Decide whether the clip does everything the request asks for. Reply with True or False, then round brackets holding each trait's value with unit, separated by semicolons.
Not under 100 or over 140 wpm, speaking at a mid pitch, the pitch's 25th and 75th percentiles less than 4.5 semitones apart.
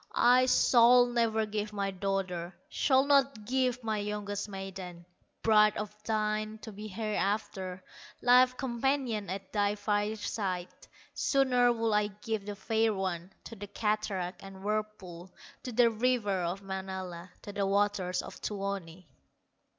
False (135 wpm; 210 Hz; 2.8 semitones)